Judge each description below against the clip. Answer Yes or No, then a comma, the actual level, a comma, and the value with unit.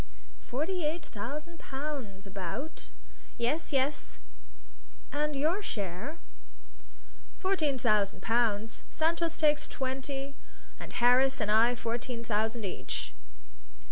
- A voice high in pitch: Yes, very high, 265 Hz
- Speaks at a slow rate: Yes, slow, 100 wpm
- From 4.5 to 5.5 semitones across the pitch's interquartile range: Yes, average, 5.2 semitones